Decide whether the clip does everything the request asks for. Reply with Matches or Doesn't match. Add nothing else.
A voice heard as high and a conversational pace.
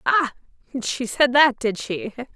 Matches